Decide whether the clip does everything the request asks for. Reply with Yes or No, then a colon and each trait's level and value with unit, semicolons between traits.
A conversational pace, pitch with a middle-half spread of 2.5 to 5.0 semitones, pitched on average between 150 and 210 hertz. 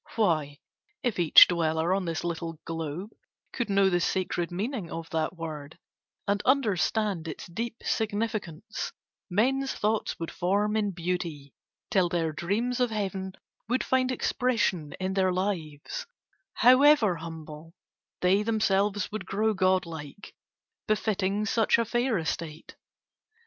No: slow, 130 wpm; average, 4.7 semitones; high, 190 Hz